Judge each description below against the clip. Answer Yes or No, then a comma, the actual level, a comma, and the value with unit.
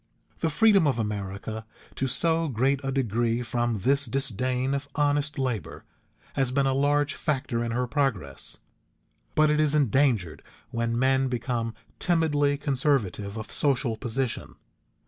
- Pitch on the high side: No, low, 130 Hz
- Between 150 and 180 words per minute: No, average, 140 wpm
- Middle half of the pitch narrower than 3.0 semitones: No, average, 3.7 semitones